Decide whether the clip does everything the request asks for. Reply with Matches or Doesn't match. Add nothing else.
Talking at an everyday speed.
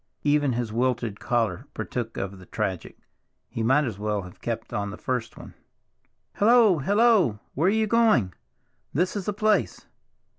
Matches